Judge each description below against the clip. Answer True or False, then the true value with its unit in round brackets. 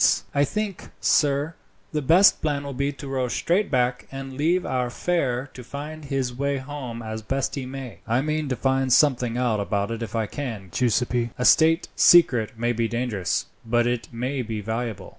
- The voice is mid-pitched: False (130 Hz)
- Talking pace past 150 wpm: True (190 wpm)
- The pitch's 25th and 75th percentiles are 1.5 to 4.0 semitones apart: True (3.2 semitones)